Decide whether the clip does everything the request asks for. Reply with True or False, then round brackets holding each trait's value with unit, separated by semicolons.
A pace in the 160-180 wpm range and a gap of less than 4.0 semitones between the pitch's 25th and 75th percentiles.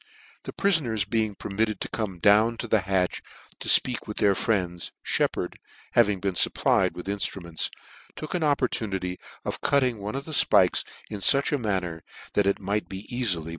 True (170 wpm; 3.6 semitones)